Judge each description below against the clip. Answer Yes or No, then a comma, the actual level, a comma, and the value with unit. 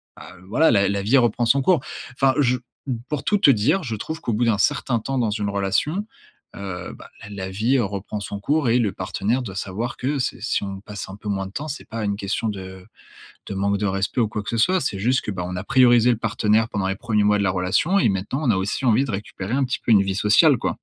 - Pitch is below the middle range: Yes, low, 105 Hz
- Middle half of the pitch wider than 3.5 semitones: Yes, average, 4.2 semitones